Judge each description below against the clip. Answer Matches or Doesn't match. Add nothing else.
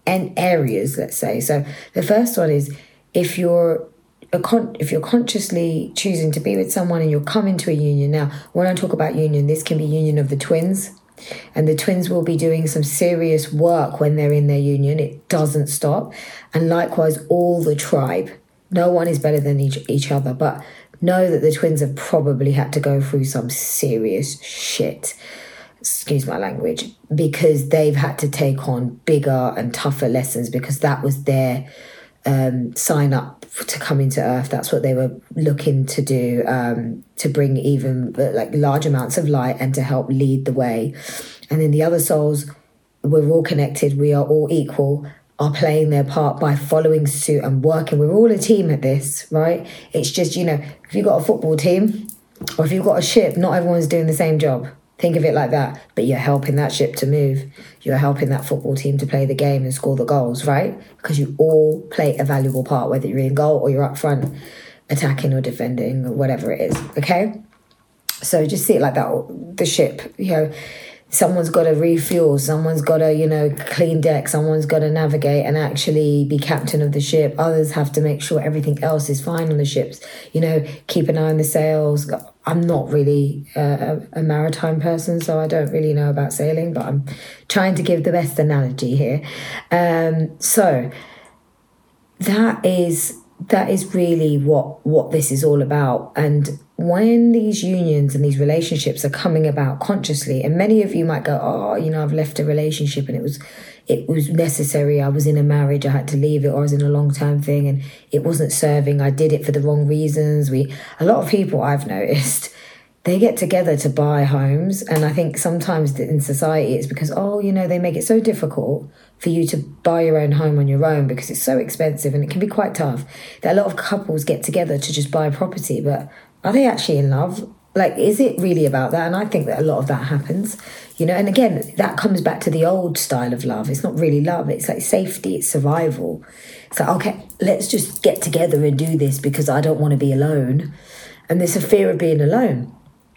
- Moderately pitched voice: Matches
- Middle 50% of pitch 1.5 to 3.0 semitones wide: Matches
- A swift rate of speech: Matches